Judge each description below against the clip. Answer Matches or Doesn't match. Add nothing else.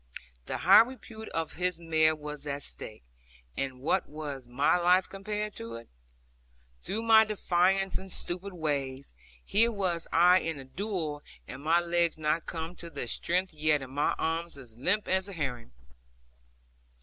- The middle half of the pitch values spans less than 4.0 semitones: Doesn't match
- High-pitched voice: Doesn't match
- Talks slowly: Doesn't match